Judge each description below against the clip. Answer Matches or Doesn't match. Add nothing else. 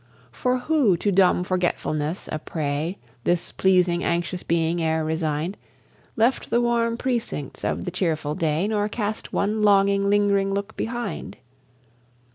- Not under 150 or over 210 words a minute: Doesn't match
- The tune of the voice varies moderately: Matches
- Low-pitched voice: Doesn't match